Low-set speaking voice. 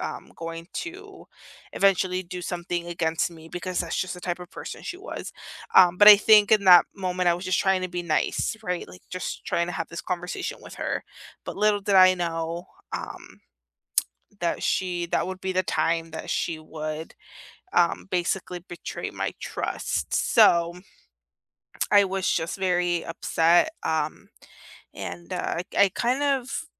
No: medium, 180 Hz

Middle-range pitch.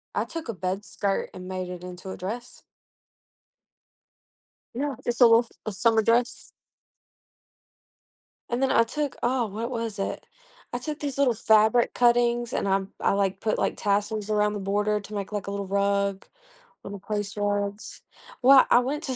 No: high, 215 Hz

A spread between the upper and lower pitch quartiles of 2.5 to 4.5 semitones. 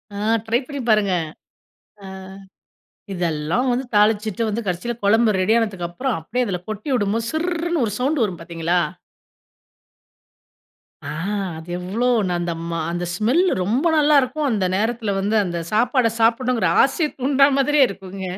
No: wide, 5.4 semitones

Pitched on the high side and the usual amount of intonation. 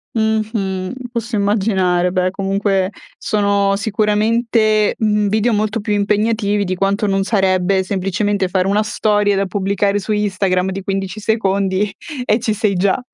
No: high, 200 Hz; narrow, 1.8 semitones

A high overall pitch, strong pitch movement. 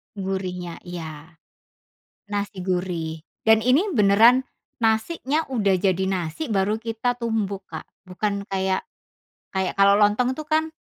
No: high, 200 Hz; average, 3.7 semitones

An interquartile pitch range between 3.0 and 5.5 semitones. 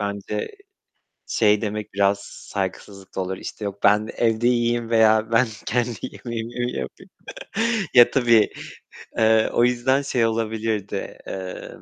No: narrow, 2.6 semitones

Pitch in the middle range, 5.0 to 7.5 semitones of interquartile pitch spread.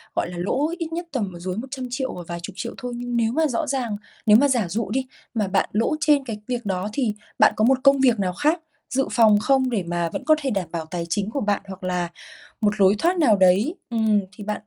No: high, 225 Hz; wide, 5.5 semitones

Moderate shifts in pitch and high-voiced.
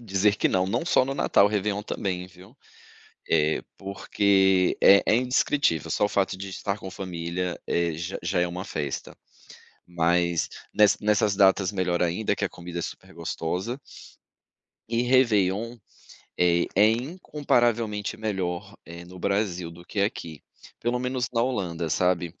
No: average, 3.5 semitones; very low, 95 Hz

